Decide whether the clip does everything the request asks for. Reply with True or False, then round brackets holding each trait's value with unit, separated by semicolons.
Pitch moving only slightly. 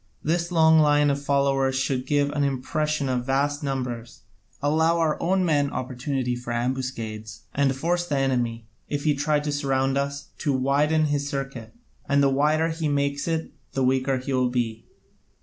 True (2.3 semitones)